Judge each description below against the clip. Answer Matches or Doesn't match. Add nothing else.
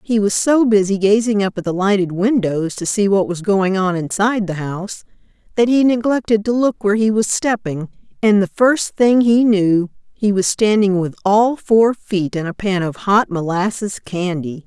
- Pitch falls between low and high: Doesn't match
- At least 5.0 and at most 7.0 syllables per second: Doesn't match